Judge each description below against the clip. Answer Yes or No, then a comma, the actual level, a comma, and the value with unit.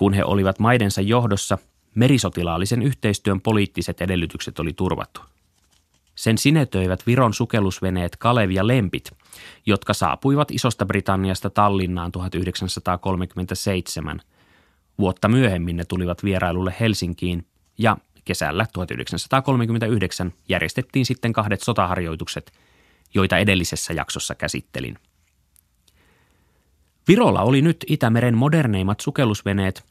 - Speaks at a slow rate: Yes, slow, 90 wpm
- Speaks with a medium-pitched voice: No, very low, 95 Hz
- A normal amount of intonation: Yes, average, 4.4 semitones